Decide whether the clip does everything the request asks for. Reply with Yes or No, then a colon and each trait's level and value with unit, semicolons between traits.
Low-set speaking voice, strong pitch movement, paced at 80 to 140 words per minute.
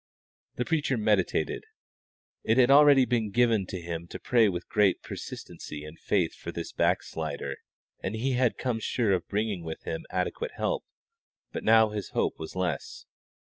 No: low, 105 Hz; wide, 5.9 semitones; average, 170 wpm